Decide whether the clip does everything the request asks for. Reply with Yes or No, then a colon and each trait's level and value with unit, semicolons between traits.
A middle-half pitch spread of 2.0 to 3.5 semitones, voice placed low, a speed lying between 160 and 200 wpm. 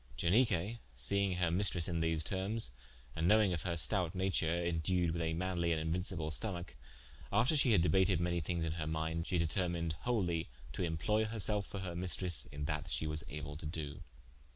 Yes: average, 2.8 semitones; very low, 85 Hz; average, 180 wpm